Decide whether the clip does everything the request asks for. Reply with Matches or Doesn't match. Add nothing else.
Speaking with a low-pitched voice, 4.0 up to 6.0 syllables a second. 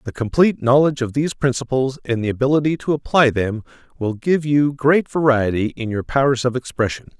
Matches